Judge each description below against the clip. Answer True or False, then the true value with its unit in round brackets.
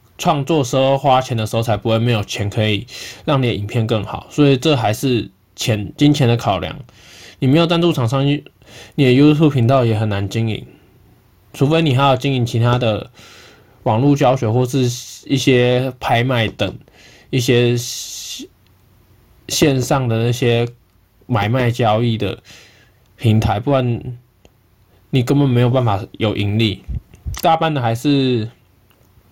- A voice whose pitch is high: False (120 Hz)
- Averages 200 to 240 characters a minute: True (225 characters per minute)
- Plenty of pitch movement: False (3.7 semitones)